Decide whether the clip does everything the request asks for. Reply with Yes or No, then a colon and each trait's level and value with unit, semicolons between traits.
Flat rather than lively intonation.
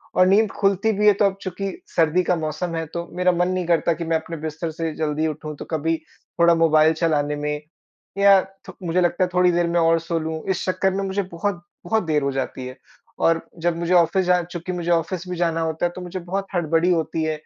Yes: narrow, 2.2 semitones